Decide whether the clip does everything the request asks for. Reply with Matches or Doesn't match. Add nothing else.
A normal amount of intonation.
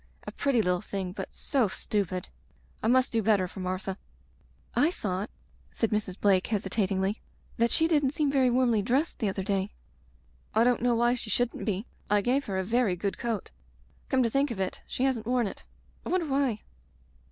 Matches